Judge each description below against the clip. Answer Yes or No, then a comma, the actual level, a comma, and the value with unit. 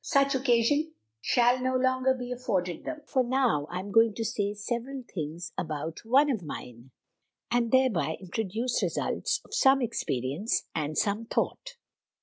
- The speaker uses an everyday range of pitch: No, wide, 6.4 semitones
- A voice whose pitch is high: Yes, high, 230 Hz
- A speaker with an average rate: Yes, average, 160 wpm